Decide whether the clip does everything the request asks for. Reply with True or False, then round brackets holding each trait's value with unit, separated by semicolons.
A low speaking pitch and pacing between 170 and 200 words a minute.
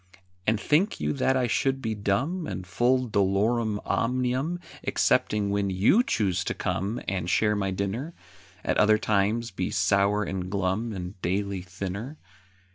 False (105 Hz; 150 wpm)